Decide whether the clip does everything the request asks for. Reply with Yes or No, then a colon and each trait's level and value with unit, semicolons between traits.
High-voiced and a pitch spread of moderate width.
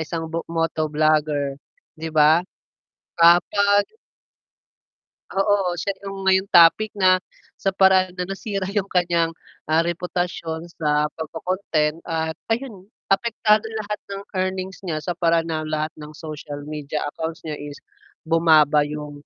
No: medium, 165 Hz; average, 3.6 semitones